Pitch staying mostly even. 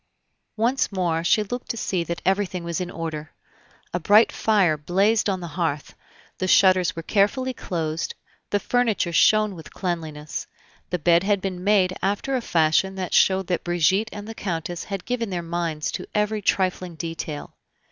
No: average, 3.5 semitones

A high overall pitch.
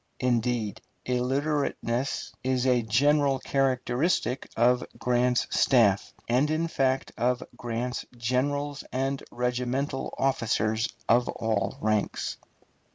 No: low, 125 Hz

